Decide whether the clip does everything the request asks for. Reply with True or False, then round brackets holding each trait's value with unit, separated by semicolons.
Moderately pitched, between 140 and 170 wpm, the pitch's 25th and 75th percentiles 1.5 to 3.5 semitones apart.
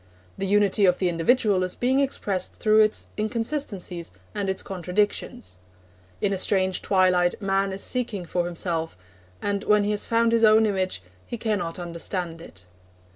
False (195 Hz; 160 wpm; 3.1 semitones)